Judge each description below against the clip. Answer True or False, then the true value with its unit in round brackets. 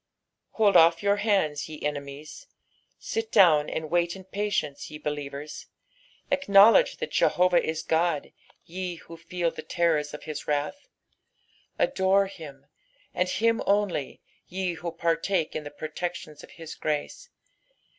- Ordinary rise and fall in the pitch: True (4.4 semitones)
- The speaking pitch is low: False (170 Hz)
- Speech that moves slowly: False (145 wpm)